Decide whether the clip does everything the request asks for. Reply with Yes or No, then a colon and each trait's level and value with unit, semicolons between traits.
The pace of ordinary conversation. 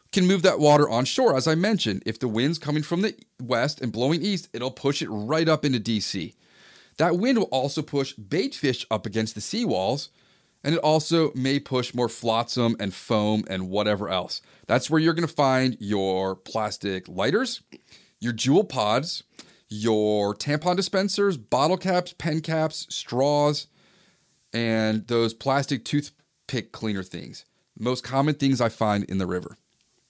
Yes: average, 165 wpm